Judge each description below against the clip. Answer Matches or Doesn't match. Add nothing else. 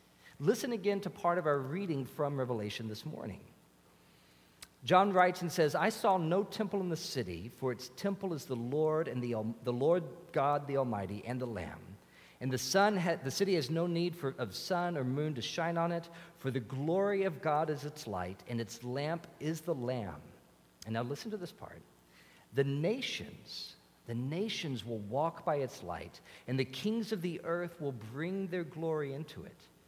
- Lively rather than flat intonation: Matches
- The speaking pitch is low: Doesn't match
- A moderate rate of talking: Matches